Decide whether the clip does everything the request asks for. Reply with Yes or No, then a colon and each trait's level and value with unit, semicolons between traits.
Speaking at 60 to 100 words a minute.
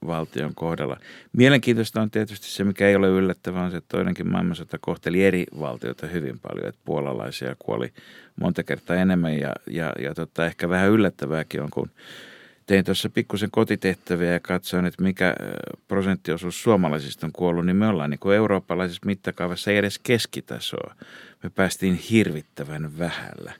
No: fast, 155 wpm